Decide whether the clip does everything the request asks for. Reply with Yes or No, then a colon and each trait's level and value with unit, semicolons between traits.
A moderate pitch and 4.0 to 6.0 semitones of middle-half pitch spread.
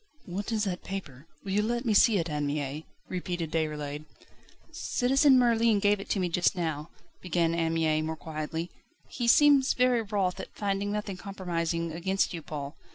Yes: medium, 180 Hz; average, 4.6 semitones